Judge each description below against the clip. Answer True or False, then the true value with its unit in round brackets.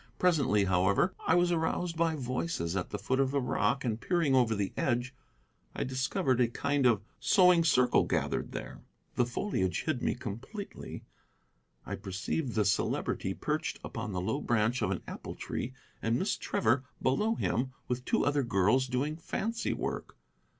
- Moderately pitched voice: False (130 Hz)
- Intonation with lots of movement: True (5.9 semitones)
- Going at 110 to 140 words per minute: False (165 wpm)